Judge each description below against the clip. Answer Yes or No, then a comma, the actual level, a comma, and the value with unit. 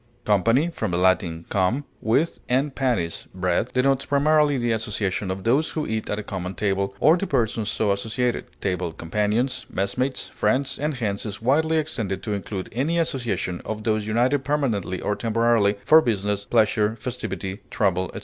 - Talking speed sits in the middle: Yes, average, 170 wpm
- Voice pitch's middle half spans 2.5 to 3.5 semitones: No, average, 4.9 semitones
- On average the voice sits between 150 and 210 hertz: No, low, 110 Hz